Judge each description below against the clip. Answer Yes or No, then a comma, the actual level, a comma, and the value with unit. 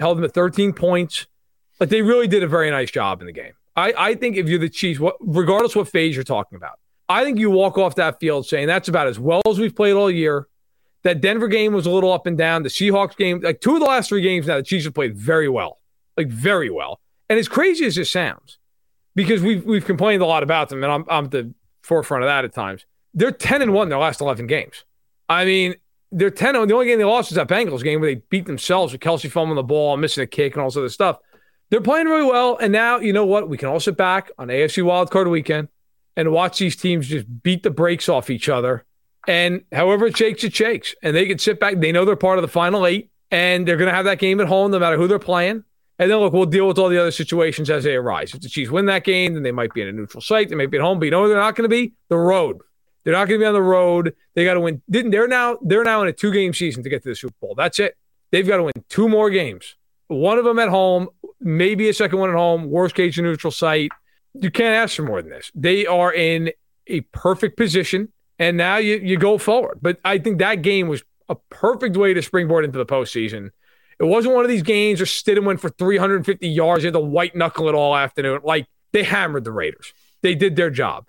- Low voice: No, medium, 180 Hz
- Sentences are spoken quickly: Yes, fast, 270 wpm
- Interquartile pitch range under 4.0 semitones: No, average, 4.3 semitones